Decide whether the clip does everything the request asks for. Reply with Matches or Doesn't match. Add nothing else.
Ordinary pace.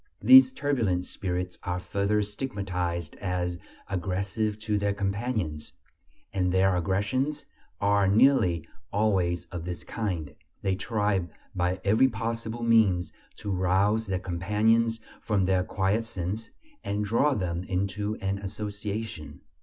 Doesn't match